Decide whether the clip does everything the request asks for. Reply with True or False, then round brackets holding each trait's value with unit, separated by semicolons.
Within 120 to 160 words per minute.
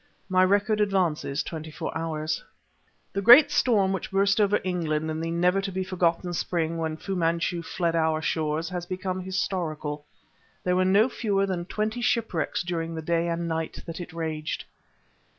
False (170 wpm)